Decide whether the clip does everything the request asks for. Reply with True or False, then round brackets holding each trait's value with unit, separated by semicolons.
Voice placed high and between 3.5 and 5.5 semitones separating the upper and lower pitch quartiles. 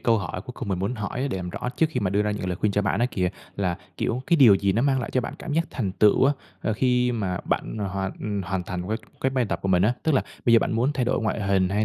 False (105 Hz; 4.5 semitones)